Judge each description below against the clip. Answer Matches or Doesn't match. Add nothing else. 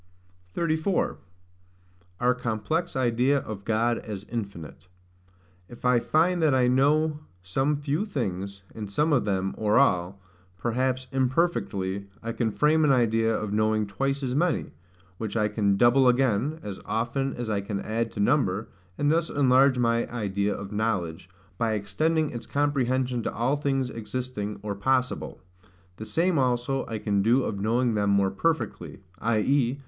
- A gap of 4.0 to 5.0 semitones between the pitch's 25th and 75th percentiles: Matches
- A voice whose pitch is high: Doesn't match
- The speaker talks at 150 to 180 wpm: Matches